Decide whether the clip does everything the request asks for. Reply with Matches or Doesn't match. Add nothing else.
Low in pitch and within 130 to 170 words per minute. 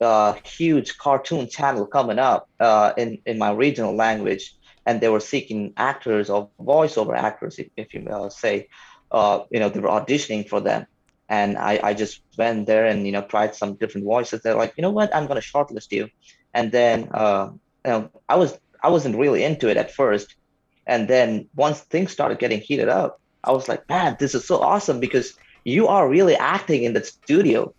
Doesn't match